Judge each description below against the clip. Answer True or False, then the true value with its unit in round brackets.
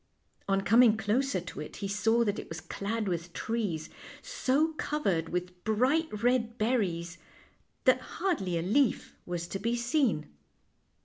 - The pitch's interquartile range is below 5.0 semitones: False (5.4 semitones)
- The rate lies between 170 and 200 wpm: False (145 wpm)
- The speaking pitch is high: True (215 Hz)